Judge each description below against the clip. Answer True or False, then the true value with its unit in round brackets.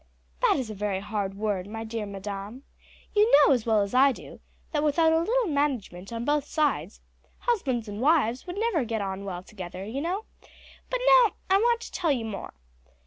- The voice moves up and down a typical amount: False (8.2 semitones)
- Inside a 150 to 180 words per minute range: False (190 wpm)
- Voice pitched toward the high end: True (245 Hz)